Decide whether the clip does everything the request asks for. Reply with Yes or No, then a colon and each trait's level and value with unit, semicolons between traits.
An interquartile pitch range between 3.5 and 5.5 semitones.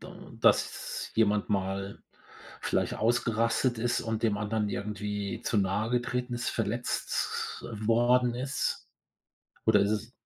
No: average, 2.8 semitones